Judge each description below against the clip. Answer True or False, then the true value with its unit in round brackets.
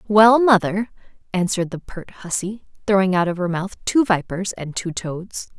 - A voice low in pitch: False (190 Hz)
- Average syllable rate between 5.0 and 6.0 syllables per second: False (4.7 syllables/s)